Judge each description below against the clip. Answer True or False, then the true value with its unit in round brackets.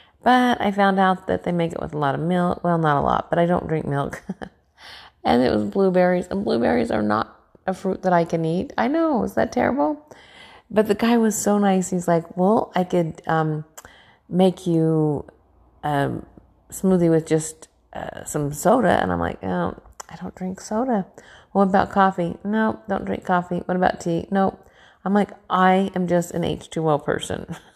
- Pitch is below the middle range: False (180 Hz)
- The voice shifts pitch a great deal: False (3.5 semitones)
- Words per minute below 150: False (195 wpm)